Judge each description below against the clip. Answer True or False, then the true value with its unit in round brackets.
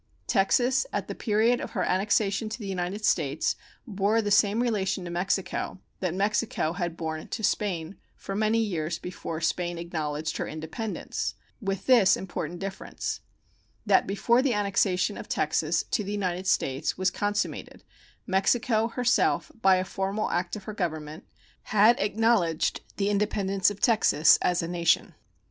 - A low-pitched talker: False (195 Hz)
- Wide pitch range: False (3.5 semitones)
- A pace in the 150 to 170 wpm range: True (155 wpm)